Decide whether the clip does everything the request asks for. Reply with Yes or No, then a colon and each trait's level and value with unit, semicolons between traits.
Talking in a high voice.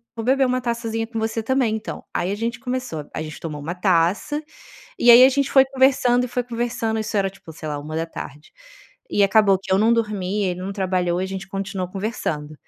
Yes: high, 210 Hz